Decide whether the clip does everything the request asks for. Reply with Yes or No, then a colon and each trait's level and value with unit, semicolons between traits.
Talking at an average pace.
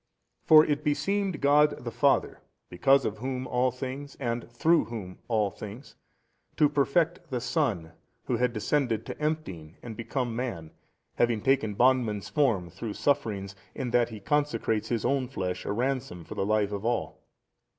Yes: average, 165 wpm